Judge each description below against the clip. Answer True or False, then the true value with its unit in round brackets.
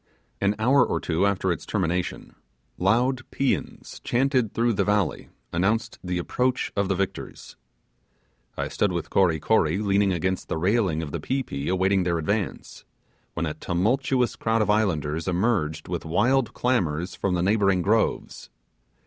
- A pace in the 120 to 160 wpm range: True (155 wpm)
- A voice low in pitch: True (100 Hz)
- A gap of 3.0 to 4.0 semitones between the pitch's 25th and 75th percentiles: False (4.4 semitones)